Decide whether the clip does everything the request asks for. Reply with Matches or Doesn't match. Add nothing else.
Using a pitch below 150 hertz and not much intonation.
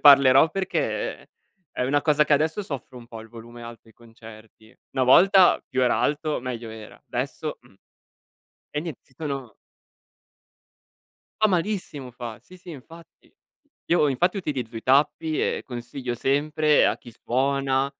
Doesn't match